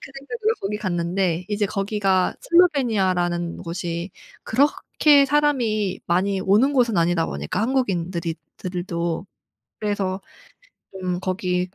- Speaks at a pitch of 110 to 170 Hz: No, high, 190 Hz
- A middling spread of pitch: Yes, average, 4.8 semitones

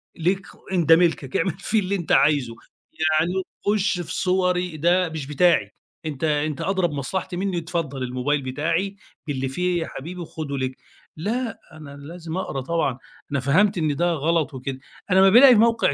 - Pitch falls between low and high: Yes, medium, 165 Hz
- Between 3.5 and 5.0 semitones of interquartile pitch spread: Yes, average, 4.1 semitones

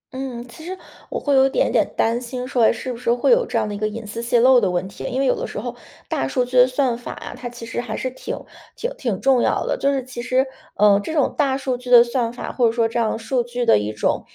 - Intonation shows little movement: Yes, narrow, 2.3 semitones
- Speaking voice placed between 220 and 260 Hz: Yes, high, 245 Hz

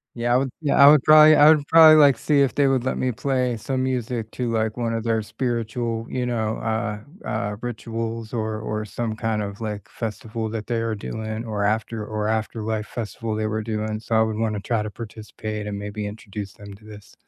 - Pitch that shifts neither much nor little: No, narrow, 2.0 semitones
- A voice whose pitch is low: Yes, low, 110 Hz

